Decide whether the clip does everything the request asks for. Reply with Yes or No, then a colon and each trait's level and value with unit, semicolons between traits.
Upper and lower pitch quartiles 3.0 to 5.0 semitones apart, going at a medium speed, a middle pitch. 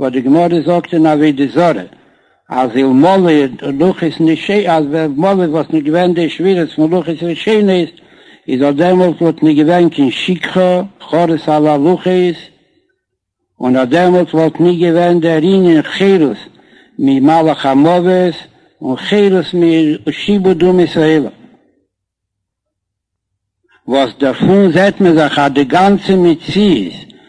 Yes: average, 3.3 semitones; average, 135 wpm; medium, 165 Hz